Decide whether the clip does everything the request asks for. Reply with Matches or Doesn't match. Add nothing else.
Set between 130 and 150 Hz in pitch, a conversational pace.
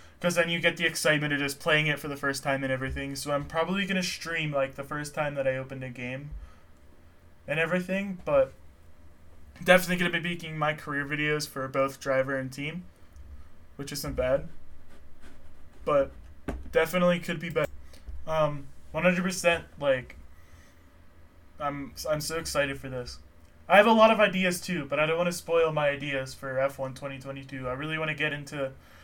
Matches